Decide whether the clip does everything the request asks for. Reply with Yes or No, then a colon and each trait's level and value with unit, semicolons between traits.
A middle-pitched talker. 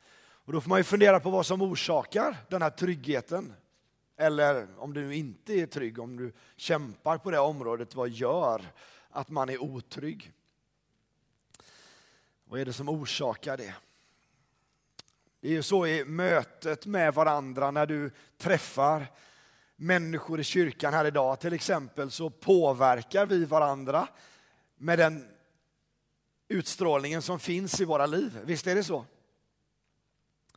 Yes: medium, 155 Hz